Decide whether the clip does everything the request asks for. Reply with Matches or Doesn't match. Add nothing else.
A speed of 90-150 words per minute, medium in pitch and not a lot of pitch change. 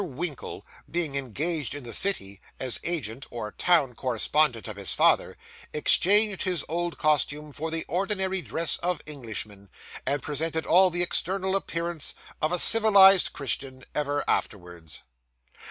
Doesn't match